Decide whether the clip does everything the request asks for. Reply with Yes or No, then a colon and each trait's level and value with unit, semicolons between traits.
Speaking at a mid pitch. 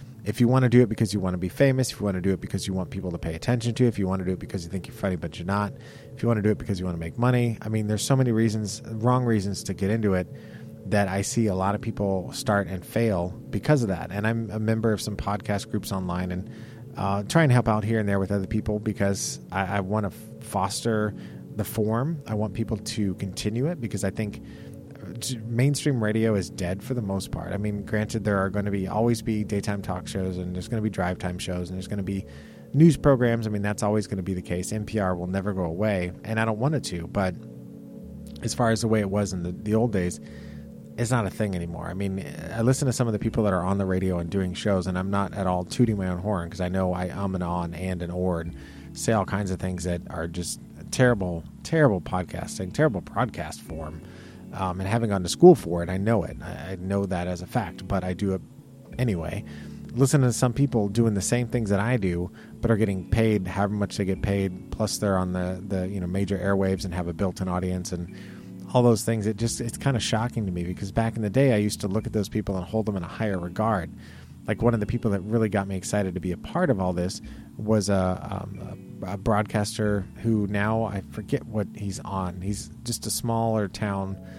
No: low, 100 Hz